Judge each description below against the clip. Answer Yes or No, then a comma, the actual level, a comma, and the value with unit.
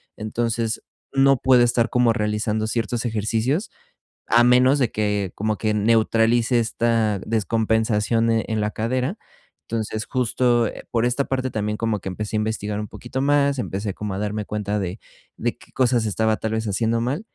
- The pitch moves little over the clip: Yes, narrow, 2.3 semitones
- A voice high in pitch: No, low, 115 Hz